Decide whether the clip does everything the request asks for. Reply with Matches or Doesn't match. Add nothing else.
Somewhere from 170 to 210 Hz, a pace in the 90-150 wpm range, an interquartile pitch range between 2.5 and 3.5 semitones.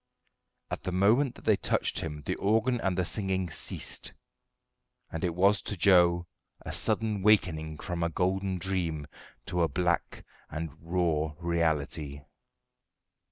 Doesn't match